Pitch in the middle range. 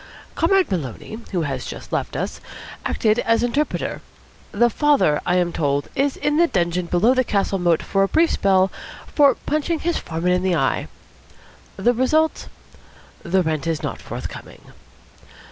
No: high, 195 Hz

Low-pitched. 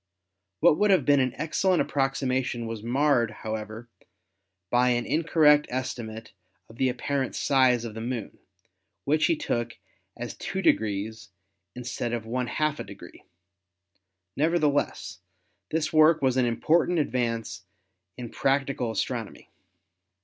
Yes: low, 125 Hz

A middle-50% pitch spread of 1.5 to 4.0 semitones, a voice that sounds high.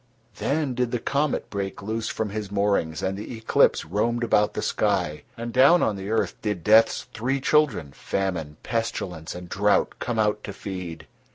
No: average, 3.4 semitones; low, 105 Hz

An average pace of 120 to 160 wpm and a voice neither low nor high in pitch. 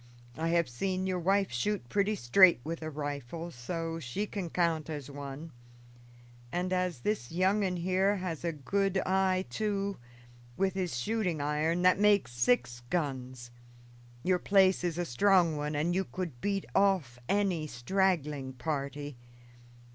Yes: average, 150 wpm; medium, 170 Hz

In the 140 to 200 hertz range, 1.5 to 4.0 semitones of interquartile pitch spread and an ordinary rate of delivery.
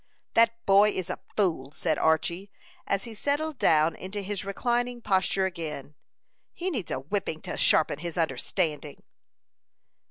No: high, 190 Hz; average, 4.9 semitones; average, 145 wpm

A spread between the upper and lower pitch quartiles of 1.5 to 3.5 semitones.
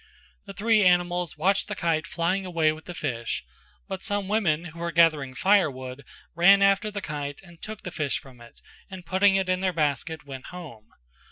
No: average, 4.1 semitones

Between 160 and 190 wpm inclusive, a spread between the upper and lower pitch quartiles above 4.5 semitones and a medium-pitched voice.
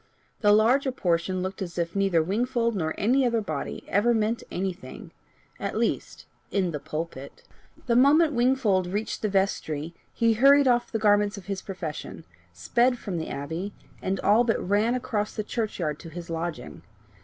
No: average, 170 wpm; average, 5.2 semitones; high, 205 Hz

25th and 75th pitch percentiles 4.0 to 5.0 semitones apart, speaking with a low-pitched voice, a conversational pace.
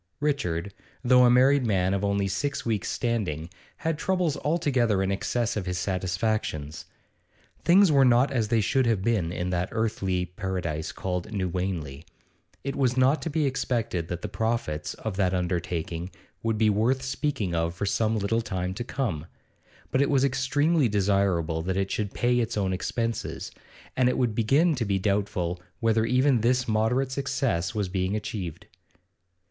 No: wide, 5.6 semitones; low, 110 Hz; average, 165 wpm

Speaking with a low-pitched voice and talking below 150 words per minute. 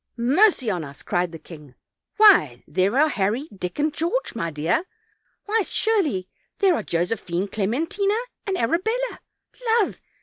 No: high, 240 Hz; average, 140 wpm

